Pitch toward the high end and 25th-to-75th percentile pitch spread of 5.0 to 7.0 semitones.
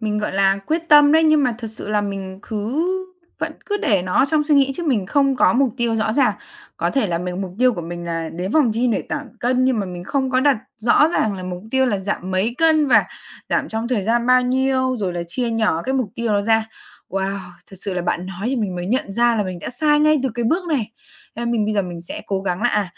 Yes: high, 225 Hz; wide, 5.4 semitones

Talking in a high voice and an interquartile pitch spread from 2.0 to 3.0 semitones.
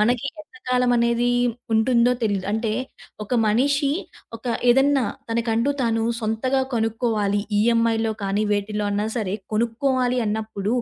Yes: high, 230 Hz; narrow, 2.5 semitones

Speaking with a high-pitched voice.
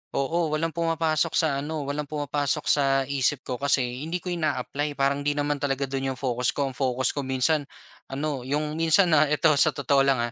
No: medium, 145 Hz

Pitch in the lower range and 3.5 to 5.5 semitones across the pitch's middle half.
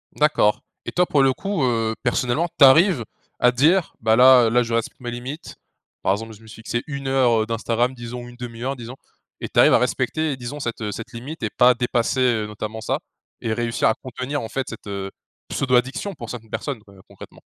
No: low, 120 Hz; average, 2.9 semitones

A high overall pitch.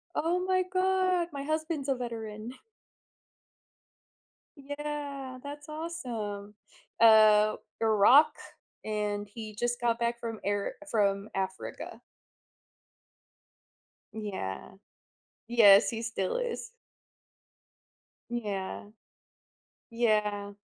Yes: high, 230 Hz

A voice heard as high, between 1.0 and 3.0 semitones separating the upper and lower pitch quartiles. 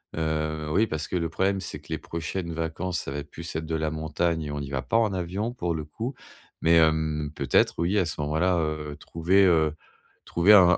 No: very low, 80 Hz; average, 2.7 semitones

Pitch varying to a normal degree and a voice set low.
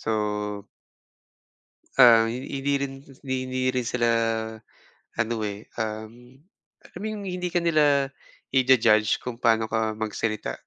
Yes: average, 3.7 semitones; low, 125 Hz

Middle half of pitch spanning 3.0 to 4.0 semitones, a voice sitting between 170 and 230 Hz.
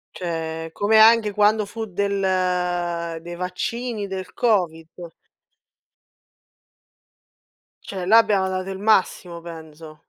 Yes: average, 3.4 semitones; medium, 185 Hz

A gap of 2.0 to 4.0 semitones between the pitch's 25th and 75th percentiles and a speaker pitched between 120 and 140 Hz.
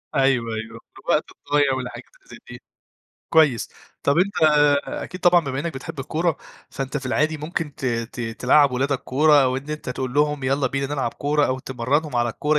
Yes: average, 2.7 semitones; low, 135 Hz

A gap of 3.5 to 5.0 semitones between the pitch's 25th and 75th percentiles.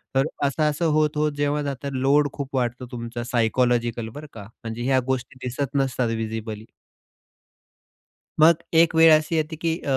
Yes: average, 4.1 semitones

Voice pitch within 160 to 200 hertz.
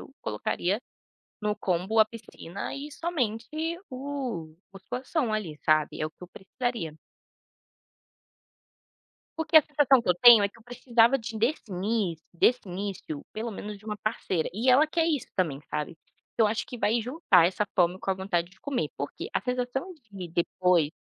No: high, 215 Hz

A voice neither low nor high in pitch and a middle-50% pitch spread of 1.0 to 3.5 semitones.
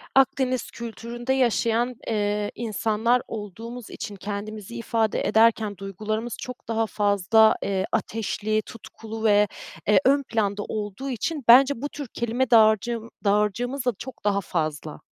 No: high, 220 Hz; narrow, 2.6 semitones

